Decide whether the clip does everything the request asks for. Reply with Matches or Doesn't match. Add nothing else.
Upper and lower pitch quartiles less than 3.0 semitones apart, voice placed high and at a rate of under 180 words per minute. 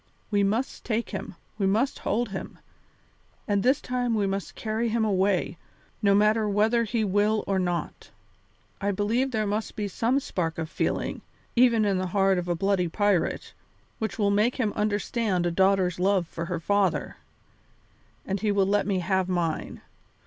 Matches